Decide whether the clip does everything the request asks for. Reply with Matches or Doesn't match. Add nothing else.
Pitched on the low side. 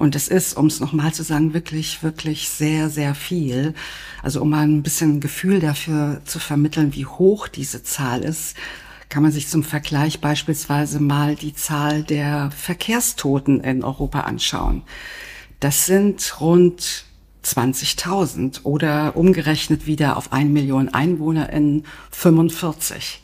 Doesn't match